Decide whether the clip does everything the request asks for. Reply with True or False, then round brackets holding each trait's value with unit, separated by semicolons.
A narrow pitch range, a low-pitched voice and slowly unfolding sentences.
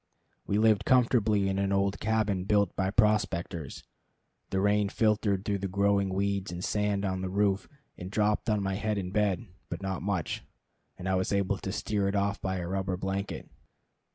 False (1.5 semitones; 100 Hz; 185 wpm)